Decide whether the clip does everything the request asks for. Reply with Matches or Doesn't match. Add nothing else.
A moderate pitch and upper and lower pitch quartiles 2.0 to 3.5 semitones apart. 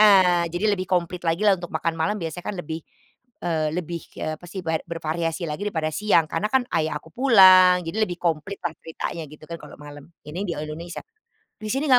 Matches